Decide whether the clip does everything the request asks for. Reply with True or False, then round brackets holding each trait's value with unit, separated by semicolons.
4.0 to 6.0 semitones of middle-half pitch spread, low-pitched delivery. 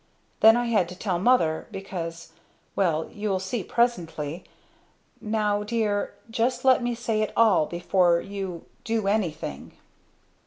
False (4.5 semitones; 200 Hz)